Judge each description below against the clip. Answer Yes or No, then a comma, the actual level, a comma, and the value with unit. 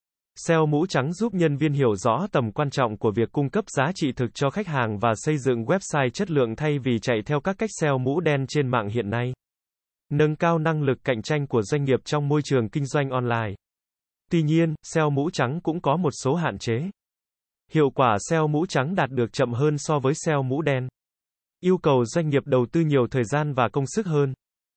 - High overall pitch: No, medium, 145 Hz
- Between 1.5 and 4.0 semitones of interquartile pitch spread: Yes, average, 3.7 semitones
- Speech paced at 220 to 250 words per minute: Yes, average, 225 wpm